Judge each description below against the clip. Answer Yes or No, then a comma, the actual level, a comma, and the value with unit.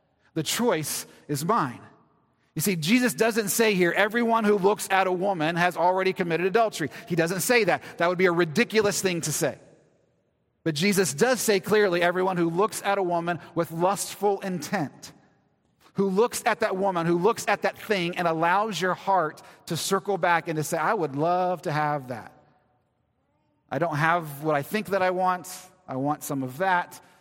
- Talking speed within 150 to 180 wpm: No, average, 190 wpm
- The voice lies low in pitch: No, medium, 185 Hz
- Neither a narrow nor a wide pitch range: Yes, average, 3.4 semitones